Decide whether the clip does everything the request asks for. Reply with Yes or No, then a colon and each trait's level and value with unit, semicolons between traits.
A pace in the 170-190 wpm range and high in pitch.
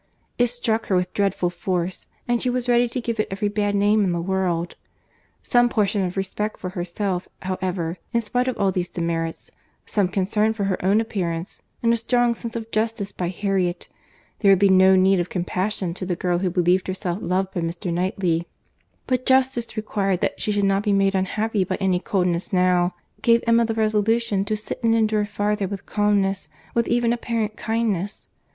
Yes: average, 185 wpm; high, 200 Hz